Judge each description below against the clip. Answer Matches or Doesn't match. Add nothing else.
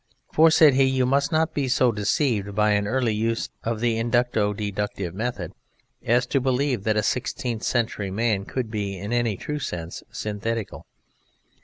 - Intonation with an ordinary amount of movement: Matches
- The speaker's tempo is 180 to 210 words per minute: Doesn't match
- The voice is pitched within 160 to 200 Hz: Doesn't match